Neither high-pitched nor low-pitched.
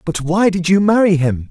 Yes: medium, 175 Hz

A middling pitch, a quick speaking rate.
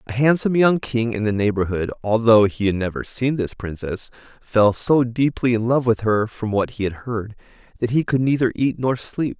No: low, 115 Hz; fast, 210 wpm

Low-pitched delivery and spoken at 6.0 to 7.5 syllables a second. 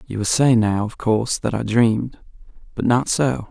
No: low, 115 Hz; 4.9 syllables/s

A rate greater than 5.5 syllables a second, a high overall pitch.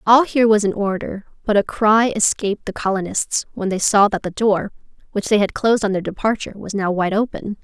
Yes: 5.8 syllables/s; high, 205 Hz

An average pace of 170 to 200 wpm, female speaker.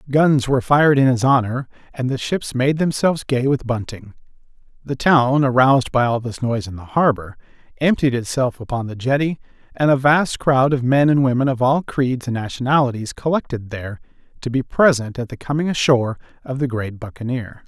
No: average, 185 wpm; male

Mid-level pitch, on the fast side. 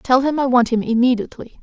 No: high, 245 Hz; fast, 220 wpm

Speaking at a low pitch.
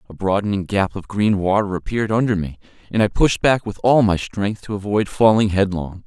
Yes: low, 100 Hz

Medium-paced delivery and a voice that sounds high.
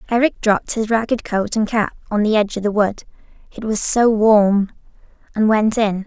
Yes: average, 180 wpm; high, 215 Hz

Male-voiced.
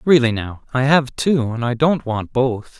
Yes: male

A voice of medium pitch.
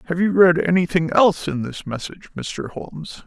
Yes: medium, 165 Hz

